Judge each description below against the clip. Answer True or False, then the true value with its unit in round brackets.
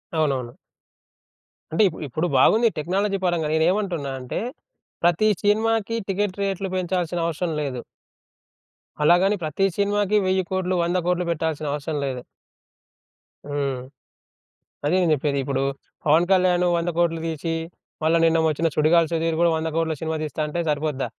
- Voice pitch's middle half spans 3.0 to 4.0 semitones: True (3.4 semitones)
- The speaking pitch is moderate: True (165 Hz)